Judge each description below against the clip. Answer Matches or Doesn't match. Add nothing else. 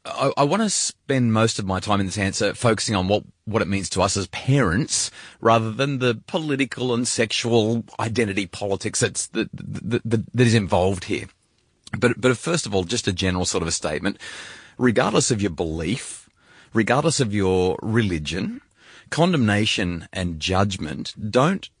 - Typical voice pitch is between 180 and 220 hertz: Doesn't match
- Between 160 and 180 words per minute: Matches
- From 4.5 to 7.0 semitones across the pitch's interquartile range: Doesn't match